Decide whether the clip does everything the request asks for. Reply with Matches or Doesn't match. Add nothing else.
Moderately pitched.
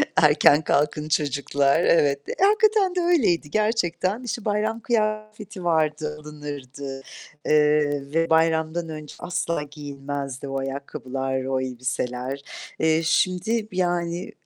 Matches